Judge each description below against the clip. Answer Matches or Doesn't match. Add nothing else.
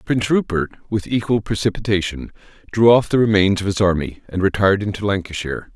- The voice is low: Matches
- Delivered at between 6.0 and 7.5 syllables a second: Matches